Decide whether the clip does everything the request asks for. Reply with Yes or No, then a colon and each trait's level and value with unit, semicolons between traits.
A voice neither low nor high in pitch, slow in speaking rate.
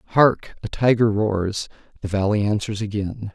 No: low, 105 Hz; slow, 125 wpm